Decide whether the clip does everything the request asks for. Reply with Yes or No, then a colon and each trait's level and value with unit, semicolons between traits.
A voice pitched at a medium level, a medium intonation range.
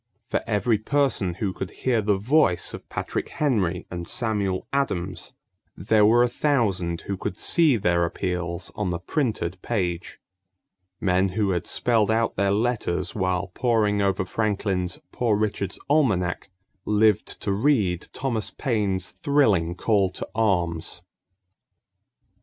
No: low, 100 Hz; average, 3.9 semitones